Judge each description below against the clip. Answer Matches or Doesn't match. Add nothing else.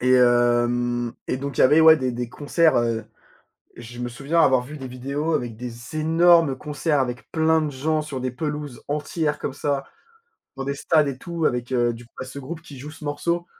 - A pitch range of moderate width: Matches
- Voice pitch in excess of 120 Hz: Matches